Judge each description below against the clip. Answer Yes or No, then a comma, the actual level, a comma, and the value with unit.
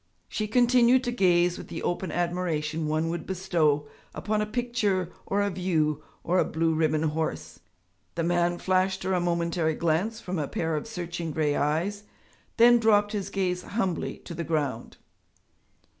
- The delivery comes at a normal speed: Yes, average, 165 wpm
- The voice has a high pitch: No, medium, 175 Hz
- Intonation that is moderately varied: Yes, average, 3.9 semitones